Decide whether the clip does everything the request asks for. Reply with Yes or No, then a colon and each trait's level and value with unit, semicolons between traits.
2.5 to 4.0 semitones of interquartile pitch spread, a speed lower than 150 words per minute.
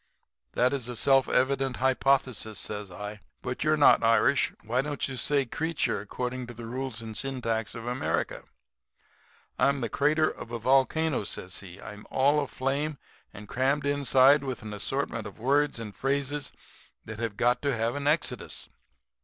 No: average, 3.7 semitones; average, 160 wpm